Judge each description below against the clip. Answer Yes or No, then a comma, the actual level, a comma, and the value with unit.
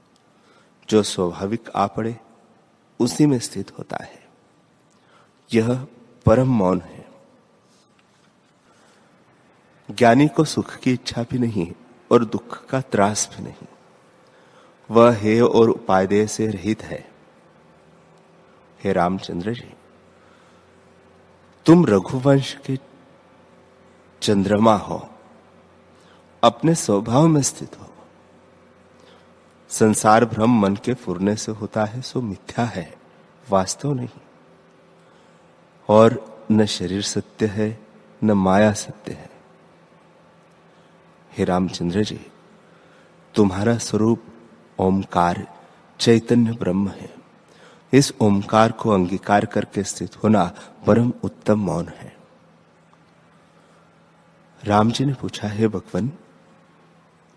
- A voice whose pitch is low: Yes, low, 115 Hz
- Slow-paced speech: Yes, slow, 95 wpm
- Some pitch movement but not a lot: Yes, average, 4.9 semitones